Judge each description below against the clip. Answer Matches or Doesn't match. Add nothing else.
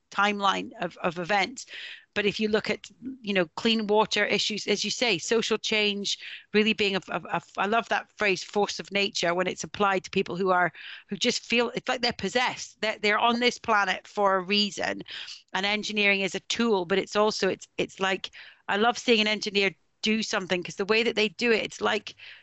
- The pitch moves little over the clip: Matches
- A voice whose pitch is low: Doesn't match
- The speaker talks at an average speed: Doesn't match